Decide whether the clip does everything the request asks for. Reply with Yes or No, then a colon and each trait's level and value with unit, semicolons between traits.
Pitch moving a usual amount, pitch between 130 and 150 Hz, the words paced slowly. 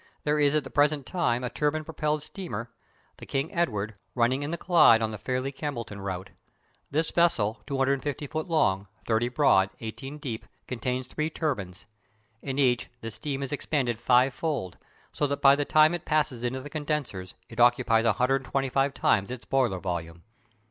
No: average, 4.5 semitones; low, 135 Hz; average, 170 wpm